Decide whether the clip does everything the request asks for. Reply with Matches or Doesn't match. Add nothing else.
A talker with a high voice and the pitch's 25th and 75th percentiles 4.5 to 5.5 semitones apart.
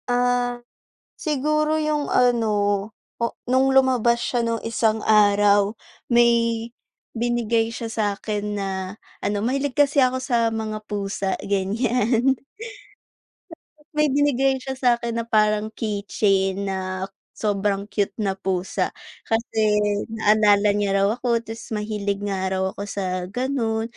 Doesn't match